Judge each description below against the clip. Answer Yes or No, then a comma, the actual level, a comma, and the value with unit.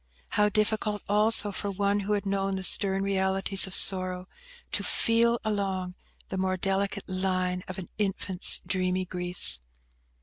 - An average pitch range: No, narrow, 1.5 semitones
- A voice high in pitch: Yes, high, 195 Hz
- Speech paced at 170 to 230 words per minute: No, average, 145 wpm